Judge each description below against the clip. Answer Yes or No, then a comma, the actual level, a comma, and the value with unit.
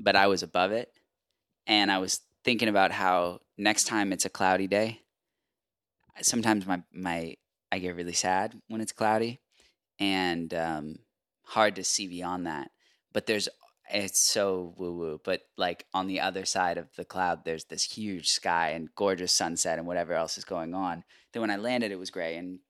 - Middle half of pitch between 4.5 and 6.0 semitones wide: No, average, 2.7 semitones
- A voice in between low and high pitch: No, very low, 95 Hz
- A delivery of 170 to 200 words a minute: Yes, average, 185 wpm